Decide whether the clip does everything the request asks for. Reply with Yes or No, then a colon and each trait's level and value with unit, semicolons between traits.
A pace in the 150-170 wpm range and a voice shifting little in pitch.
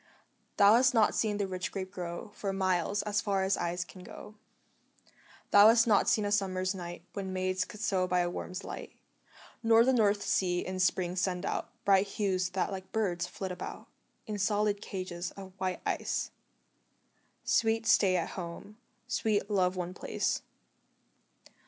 Yes: average, 165 wpm; narrow, 2.1 semitones